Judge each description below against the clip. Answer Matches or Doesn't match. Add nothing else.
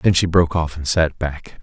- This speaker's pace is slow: Doesn't match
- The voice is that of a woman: Doesn't match